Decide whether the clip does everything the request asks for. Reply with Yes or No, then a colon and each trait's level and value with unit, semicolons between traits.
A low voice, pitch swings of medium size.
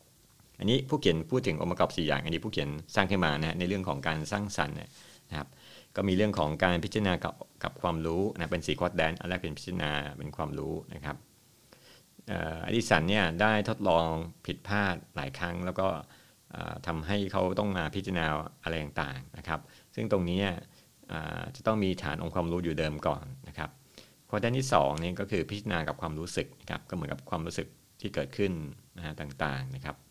Yes: very low, 85 Hz; average, 4.3 semitones